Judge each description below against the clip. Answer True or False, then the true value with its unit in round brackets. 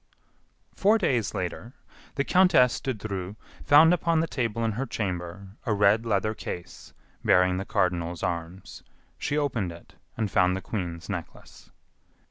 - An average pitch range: False (5.7 semitones)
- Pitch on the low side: True (105 Hz)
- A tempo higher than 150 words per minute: False (145 wpm)